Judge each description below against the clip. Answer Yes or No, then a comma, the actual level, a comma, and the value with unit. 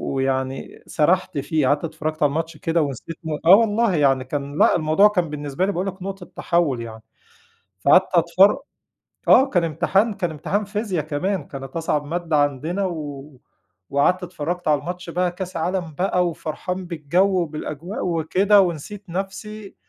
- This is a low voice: No, medium, 170 Hz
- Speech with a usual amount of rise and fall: Yes, average, 4.0 semitones